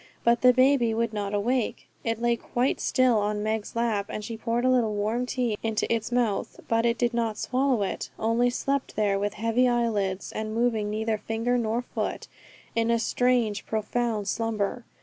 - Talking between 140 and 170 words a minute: No, average, 185 wpm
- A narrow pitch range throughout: Yes, narrow, 2.2 semitones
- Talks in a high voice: Yes, high, 230 Hz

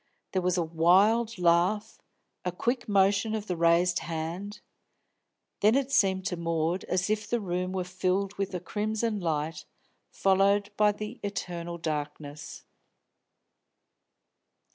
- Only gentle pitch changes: No, average, 3.4 semitones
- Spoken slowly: Yes, slow, 130 wpm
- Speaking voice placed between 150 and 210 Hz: Yes, medium, 185 Hz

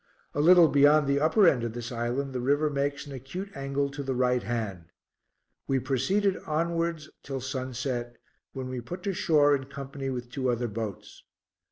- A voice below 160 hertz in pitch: Yes, low, 135 Hz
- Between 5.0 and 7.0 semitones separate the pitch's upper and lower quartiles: No, average, 3.1 semitones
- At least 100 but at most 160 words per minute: No, average, 180 wpm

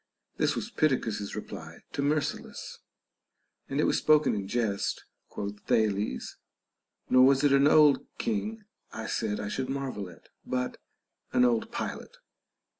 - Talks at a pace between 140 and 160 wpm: Yes, average, 145 wpm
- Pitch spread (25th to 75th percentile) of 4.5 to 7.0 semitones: Yes, average, 5.3 semitones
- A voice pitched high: No, low, 125 Hz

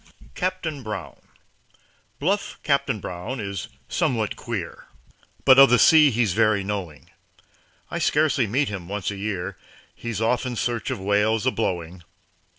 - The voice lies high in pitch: No, low, 110 Hz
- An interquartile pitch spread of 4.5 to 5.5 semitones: Yes, average, 4.8 semitones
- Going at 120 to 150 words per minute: Yes, average, 145 wpm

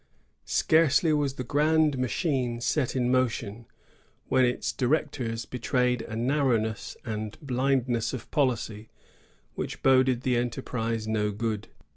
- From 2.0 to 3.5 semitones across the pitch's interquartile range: Yes, average, 2.9 semitones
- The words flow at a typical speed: No, slow, 120 wpm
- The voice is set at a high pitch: No, low, 125 Hz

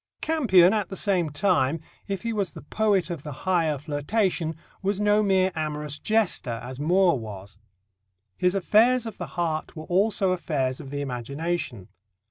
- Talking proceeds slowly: No, average, 160 wpm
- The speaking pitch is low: No, medium, 175 Hz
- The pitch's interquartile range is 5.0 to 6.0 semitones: Yes, average, 5.3 semitones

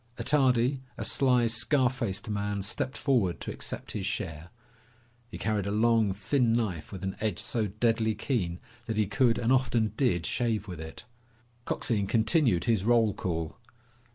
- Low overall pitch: Yes, low, 110 Hz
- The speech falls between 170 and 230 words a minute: No, average, 160 wpm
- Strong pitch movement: No, average, 3.7 semitones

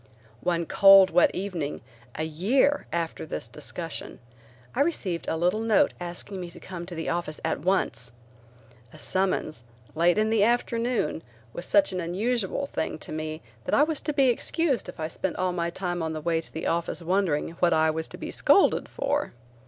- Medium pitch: Yes, medium, 175 Hz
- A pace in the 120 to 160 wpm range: No, average, 190 wpm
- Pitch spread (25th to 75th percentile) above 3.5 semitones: Yes, average, 4.6 semitones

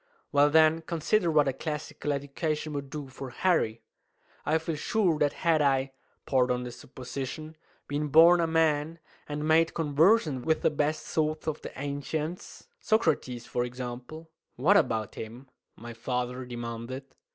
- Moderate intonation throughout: Yes, average, 3.7 semitones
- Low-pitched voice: No, medium, 145 Hz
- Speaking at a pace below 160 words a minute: Yes, average, 150 wpm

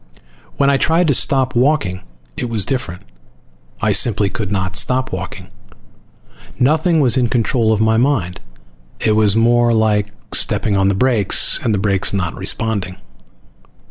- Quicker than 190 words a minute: No, average, 150 wpm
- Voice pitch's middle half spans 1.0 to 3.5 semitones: No, average, 4.4 semitones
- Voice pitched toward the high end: No, low, 110 Hz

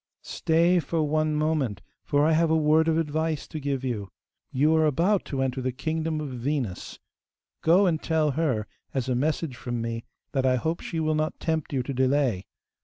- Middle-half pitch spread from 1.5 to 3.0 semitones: No, average, 3.6 semitones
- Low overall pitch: No, medium, 150 Hz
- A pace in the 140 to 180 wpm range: No, average, 195 wpm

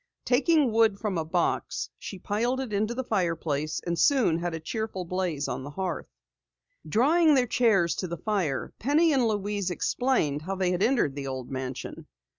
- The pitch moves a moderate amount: No, wide, 6.2 semitones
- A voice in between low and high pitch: No, high, 195 Hz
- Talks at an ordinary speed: Yes, average, 180 wpm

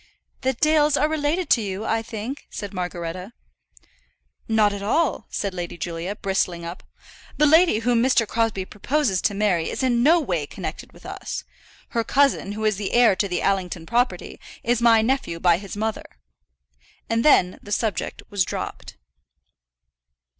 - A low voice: No, high, 215 Hz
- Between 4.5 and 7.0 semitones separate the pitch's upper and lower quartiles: Yes, average, 4.8 semitones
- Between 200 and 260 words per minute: No, average, 160 wpm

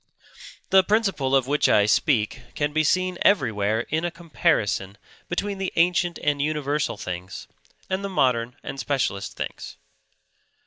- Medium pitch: Yes, medium, 145 Hz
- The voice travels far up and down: Yes, wide, 7.2 semitones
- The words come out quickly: No, average, 140 wpm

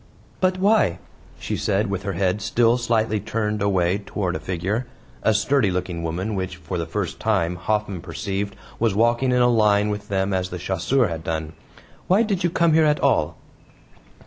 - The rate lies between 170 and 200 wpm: Yes, average, 185 wpm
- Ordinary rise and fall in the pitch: Yes, average, 4.4 semitones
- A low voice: Yes, low, 100 Hz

